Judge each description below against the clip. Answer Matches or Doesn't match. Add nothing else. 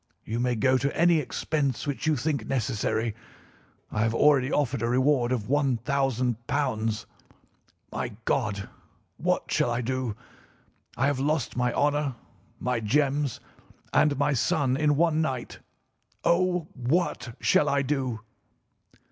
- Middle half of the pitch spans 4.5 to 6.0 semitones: Doesn't match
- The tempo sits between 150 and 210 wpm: Doesn't match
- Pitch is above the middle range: Doesn't match